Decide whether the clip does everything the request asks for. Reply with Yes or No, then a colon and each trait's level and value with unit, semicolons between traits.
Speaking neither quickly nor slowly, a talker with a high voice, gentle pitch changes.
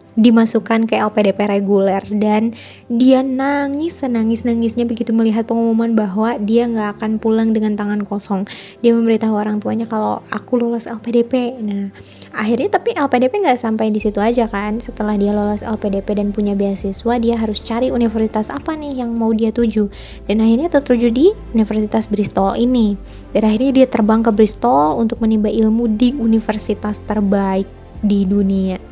No: fast, 160 wpm; high, 225 Hz; narrow, 2.0 semitones